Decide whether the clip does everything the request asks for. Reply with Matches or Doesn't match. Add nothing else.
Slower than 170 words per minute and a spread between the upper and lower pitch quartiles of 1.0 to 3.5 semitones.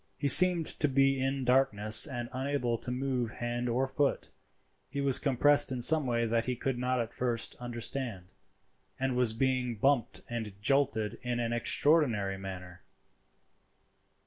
Matches